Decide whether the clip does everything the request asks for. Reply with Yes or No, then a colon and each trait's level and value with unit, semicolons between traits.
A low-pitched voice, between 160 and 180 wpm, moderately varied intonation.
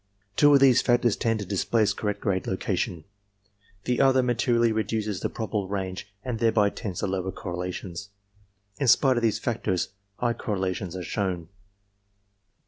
No: low, 105 Hz; average, 150 wpm; average, 4.1 semitones